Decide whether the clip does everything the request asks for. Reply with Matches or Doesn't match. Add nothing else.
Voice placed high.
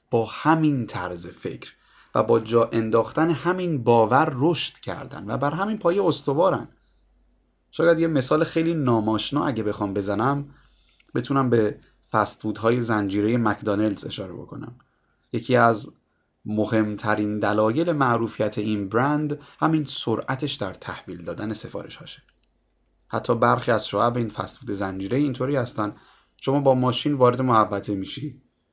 Doesn't match